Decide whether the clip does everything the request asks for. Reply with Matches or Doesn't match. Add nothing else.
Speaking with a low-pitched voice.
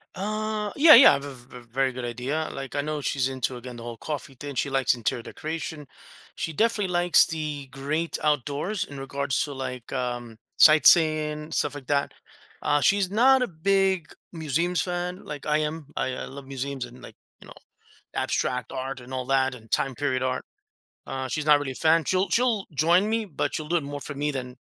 Doesn't match